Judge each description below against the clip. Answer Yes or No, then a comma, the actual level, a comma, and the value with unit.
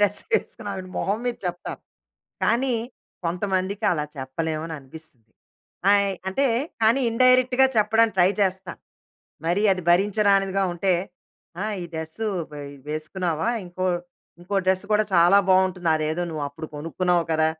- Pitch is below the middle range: No, medium, 185 Hz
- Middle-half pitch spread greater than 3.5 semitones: Yes, average, 4.1 semitones